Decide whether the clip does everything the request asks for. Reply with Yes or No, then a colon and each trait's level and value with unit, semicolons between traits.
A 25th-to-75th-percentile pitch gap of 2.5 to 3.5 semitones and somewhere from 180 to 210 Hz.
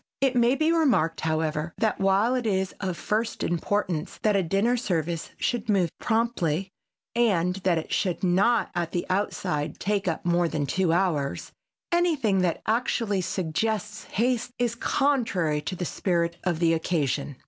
No: average, 5.1 semitones; high, 190 Hz